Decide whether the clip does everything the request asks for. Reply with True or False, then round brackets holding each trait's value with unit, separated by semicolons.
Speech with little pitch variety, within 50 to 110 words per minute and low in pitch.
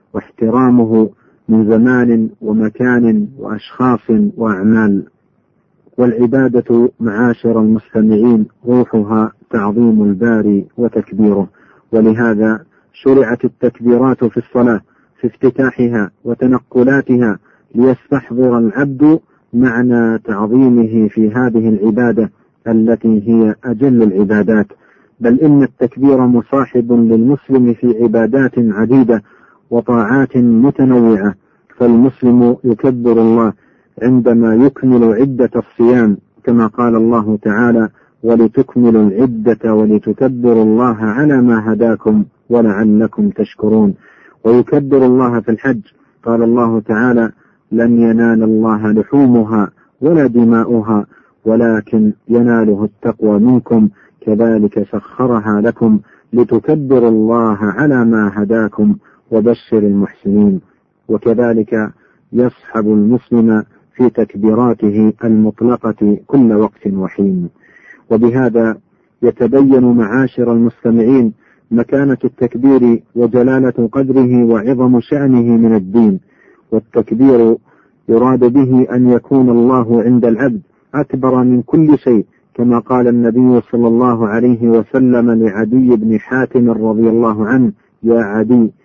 True (2.0 semitones; 95 wpm; 115 Hz)